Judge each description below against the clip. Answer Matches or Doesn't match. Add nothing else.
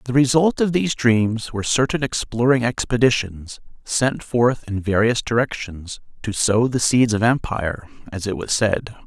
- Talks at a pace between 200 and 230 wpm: Doesn't match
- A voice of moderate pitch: Doesn't match